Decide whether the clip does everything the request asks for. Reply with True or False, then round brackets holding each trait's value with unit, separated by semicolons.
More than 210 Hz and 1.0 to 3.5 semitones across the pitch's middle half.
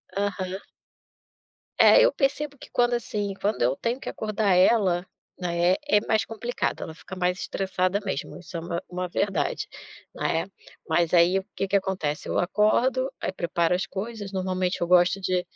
False (190 Hz; 2.9 semitones)